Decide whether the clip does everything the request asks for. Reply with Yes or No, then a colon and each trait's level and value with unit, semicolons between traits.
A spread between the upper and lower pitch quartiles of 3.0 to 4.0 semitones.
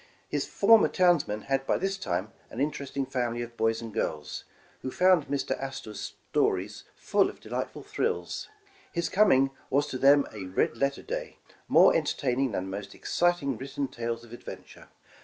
No: average, 4.6 semitones